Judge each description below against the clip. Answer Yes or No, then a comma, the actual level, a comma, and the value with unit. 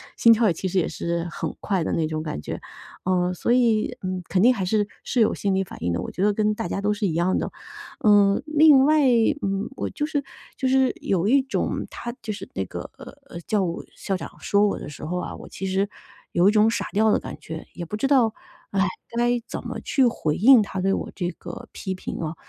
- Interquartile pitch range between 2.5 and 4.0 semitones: No, average, 4.5 semitones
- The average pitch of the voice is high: Yes, high, 200 Hz